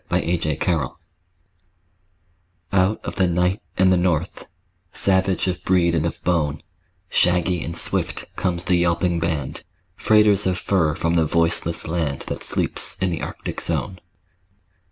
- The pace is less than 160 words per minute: Yes, average, 145 wpm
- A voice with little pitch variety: Yes, narrow, 1.9 semitones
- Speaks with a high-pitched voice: No, very low, 85 Hz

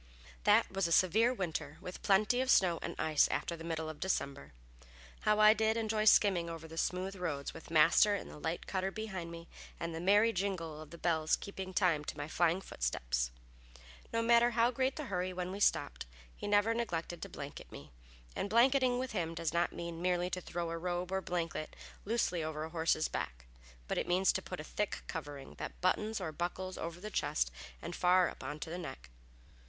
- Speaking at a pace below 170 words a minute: No, fast, 205 wpm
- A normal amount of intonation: Yes, average, 4.0 semitones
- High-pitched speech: No, medium, 180 Hz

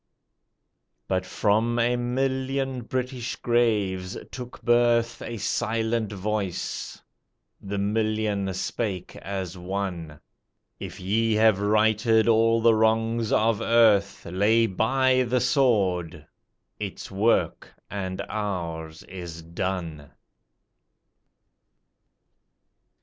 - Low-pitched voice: Yes, low, 110 Hz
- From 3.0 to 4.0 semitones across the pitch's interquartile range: Yes, average, 3.6 semitones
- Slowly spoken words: Yes, slow, 90 wpm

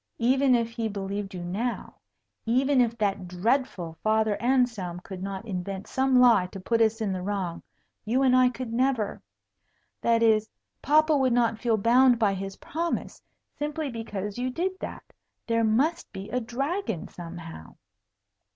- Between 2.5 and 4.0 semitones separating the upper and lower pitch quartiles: No, average, 4.5 semitones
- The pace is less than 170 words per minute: Yes, average, 160 wpm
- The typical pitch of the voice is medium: No, high, 230 Hz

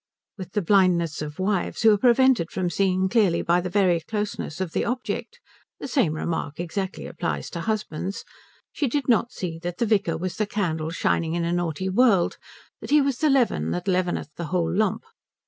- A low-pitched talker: No, medium, 185 Hz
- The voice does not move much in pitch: No, average, 4.2 semitones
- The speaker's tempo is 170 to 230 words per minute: Yes, average, 195 wpm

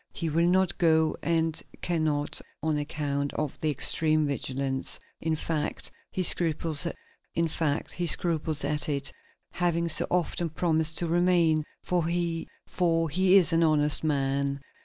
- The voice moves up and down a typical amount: No, narrow, 2.3 semitones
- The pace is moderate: No, slow, 125 wpm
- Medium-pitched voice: Yes, medium, 160 Hz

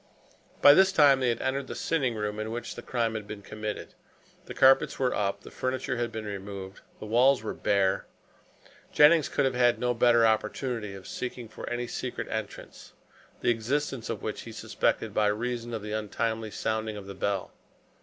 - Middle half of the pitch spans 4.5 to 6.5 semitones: No, average, 3.0 semitones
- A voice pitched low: Yes, low, 115 Hz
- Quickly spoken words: No, average, 190 wpm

